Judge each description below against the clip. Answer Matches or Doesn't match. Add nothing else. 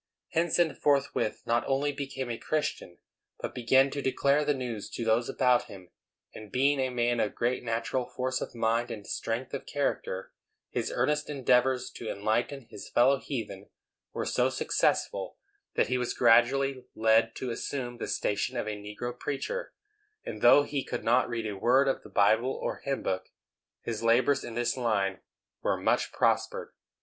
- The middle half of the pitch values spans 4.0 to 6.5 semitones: Doesn't match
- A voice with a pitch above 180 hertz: Doesn't match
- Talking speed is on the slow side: Doesn't match